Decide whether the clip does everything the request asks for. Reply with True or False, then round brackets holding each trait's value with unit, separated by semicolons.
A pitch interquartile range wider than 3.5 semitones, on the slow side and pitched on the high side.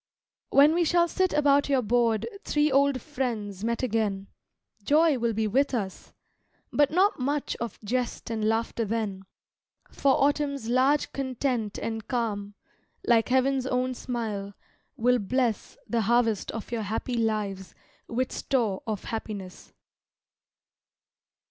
True (3.9 semitones; 130 wpm; 240 Hz)